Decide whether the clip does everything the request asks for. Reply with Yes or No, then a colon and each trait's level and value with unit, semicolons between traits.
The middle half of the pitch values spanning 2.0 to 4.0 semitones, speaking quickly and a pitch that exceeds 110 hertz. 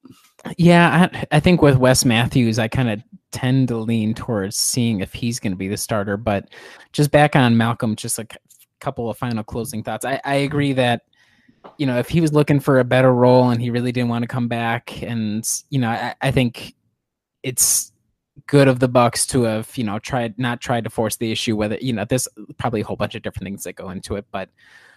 Yes: average, 2.9 semitones; fast, 230 wpm; low, 120 Hz